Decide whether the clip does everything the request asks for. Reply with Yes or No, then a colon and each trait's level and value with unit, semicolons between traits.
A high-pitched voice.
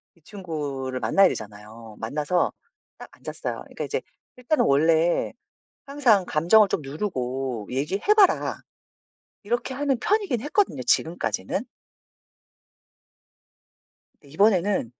No: medium, 170 Hz